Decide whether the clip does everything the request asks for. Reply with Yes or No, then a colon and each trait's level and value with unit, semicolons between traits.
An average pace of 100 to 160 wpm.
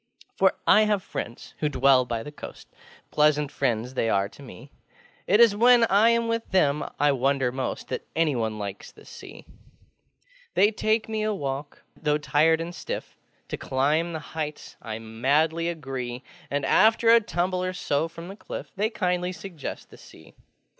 No: average, 175 wpm